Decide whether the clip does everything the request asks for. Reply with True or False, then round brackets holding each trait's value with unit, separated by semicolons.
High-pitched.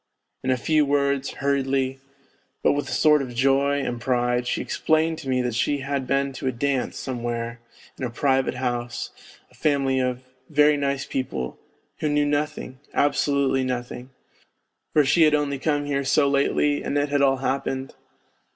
False (135 Hz)